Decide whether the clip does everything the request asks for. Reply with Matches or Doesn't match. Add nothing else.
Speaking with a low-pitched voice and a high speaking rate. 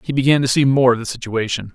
Matches